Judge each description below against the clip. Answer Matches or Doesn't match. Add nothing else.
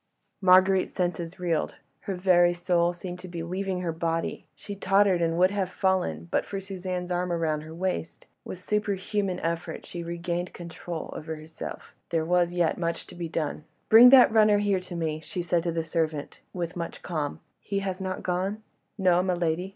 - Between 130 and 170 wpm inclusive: Doesn't match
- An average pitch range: Doesn't match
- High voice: Doesn't match